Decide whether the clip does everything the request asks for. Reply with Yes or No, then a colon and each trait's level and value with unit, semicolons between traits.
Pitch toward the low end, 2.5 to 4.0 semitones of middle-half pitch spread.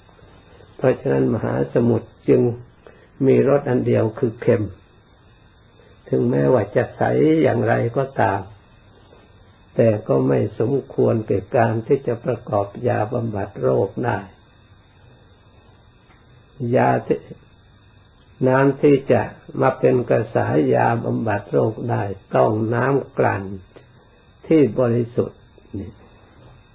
Yes: low, 115 Hz; average, 3.4 semitones